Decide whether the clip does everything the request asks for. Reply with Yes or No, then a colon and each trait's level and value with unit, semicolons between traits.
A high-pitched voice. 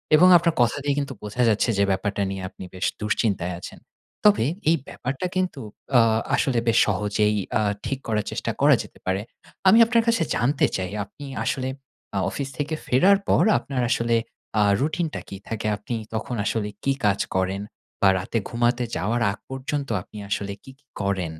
No: low, 120 Hz